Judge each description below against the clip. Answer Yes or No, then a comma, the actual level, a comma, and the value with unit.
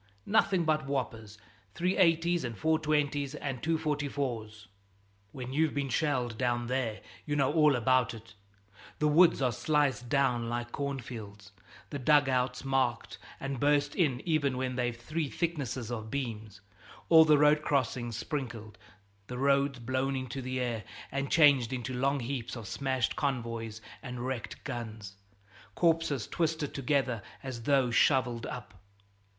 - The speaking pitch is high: No, low, 130 Hz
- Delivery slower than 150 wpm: Yes, average, 140 wpm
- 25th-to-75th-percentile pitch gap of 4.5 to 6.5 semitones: No, average, 3.5 semitones